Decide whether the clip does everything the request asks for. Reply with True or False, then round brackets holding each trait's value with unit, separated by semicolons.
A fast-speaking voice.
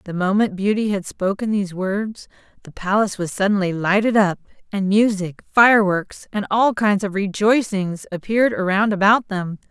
False (155 wpm)